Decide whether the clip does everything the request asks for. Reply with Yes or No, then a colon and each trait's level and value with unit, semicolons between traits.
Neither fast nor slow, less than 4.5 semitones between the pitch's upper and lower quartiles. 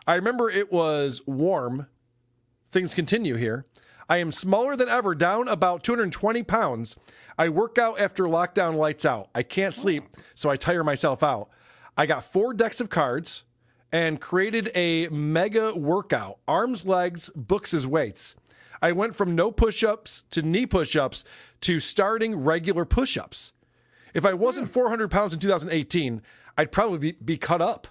No: average, 155 wpm; wide, 5.6 semitones